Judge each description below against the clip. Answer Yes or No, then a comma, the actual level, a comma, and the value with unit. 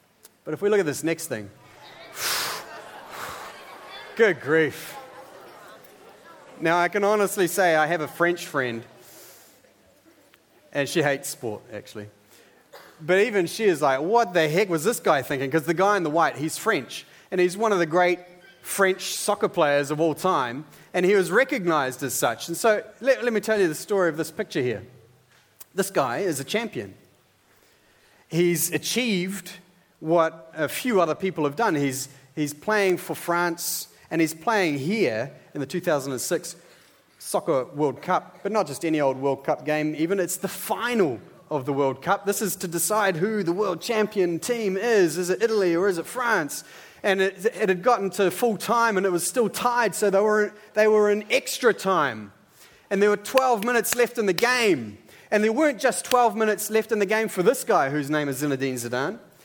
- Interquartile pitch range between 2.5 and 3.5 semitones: No, average, 5.2 semitones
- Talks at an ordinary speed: Yes, average, 190 wpm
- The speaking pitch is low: No, medium, 180 Hz